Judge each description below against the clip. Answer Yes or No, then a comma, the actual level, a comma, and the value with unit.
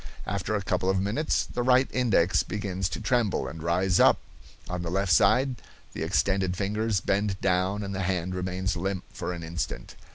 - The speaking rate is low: No, average, 185 wpm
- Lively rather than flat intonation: No, narrow, 2.4 semitones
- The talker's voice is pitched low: Yes, very low, 95 Hz